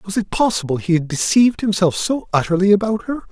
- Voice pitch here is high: Yes, high, 200 Hz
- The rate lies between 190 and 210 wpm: Yes, average, 200 wpm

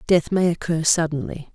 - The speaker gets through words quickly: No, average, 155 wpm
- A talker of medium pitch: Yes, medium, 160 Hz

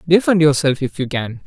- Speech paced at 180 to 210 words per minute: Yes, fast, 205 wpm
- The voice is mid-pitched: Yes, medium, 150 Hz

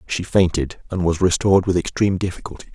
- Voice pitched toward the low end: Yes, very low, 90 Hz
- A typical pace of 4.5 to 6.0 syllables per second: No, 6.4 syllables/s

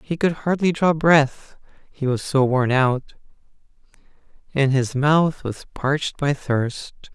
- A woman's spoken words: No, male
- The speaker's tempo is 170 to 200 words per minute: No, average, 145 wpm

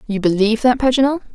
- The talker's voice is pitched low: No, high, 235 Hz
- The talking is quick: No, average, 180 wpm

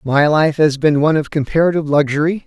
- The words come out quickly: No, average, 195 wpm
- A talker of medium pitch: Yes, medium, 150 Hz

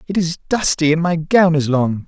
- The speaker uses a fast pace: Yes, fast, 230 wpm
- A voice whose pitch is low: No, medium, 165 Hz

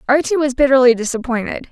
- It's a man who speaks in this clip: No, female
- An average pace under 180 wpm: Yes, average, 140 wpm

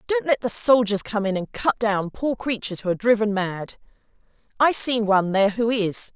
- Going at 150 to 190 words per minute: No, fast, 205 wpm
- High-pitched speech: Yes, high, 220 Hz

